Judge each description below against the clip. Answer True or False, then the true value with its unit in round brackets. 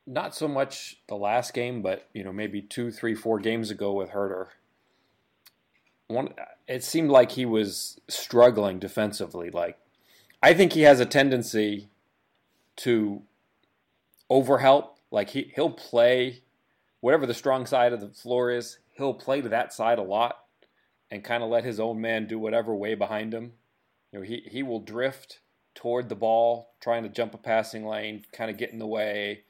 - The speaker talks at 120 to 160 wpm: False (175 wpm)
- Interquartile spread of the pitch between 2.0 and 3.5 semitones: True (2.7 semitones)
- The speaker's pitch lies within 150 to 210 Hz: False (115 Hz)